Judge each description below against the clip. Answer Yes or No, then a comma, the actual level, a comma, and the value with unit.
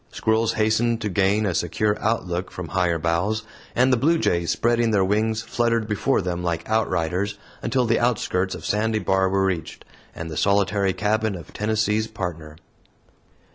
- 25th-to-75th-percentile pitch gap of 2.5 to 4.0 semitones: Yes, average, 3.6 semitones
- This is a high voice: No, low, 105 Hz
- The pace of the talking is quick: No, average, 160 wpm